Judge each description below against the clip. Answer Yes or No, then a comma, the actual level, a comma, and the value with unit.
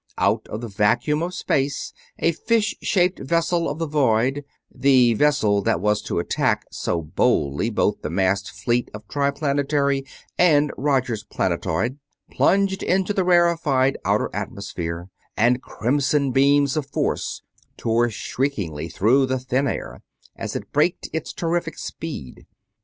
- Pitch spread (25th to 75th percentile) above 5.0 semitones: Yes, wide, 5.4 semitones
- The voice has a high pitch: No, low, 135 Hz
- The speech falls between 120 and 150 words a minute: Yes, average, 140 wpm